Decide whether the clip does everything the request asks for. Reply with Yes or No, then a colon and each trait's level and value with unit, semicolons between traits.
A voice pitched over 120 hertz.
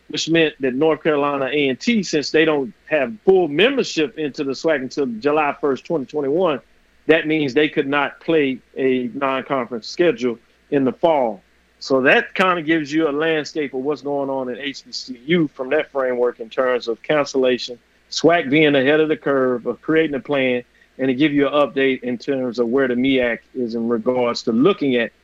Yes: medium, 140 Hz